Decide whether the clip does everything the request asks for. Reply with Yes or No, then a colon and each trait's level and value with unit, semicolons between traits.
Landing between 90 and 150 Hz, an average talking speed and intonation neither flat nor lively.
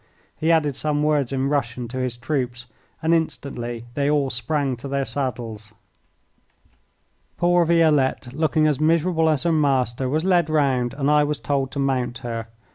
Yes: medium, 140 Hz; average, 165 wpm; average, 3.5 semitones